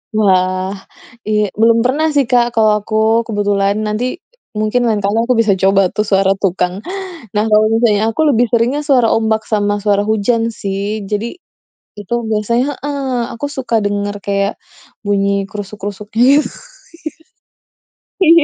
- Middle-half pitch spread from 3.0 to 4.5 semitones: No, narrow, 2.4 semitones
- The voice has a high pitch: Yes, high, 215 Hz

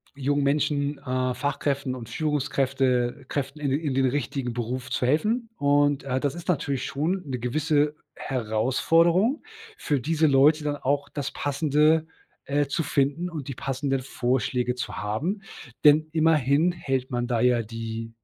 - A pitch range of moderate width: Yes, average, 3.0 semitones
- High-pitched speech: No, medium, 140 Hz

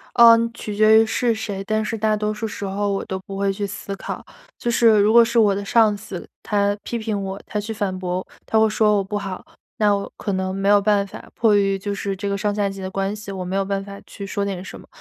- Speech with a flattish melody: Yes, narrow, 1.6 semitones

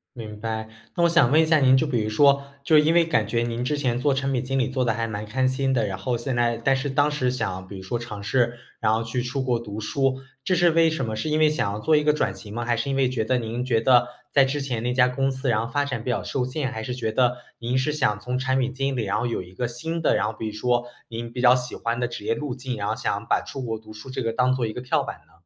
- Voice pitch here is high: No, low, 125 Hz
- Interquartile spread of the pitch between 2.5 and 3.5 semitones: Yes, average, 2.9 semitones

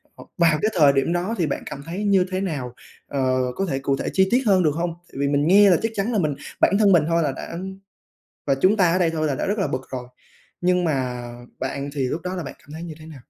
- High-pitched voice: No, medium, 165 Hz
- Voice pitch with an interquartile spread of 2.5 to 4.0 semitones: No, average, 5.0 semitones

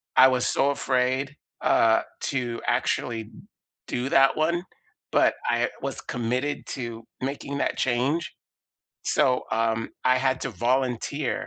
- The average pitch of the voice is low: Yes, low, 130 Hz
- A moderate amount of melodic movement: No, narrow, 2.3 semitones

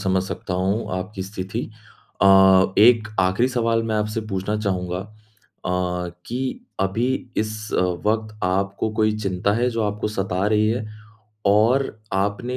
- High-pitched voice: No, low, 105 Hz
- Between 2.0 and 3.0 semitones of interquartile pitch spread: Yes, average, 2.7 semitones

